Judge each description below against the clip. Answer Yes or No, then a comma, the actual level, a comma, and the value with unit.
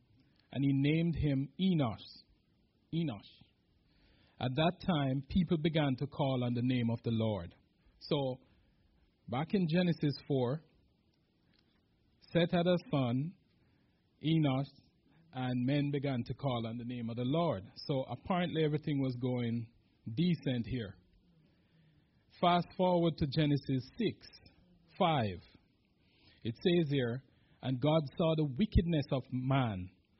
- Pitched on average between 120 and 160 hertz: Yes, low, 135 Hz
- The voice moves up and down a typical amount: Yes, average, 4.8 semitones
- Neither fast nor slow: No, slow, 125 wpm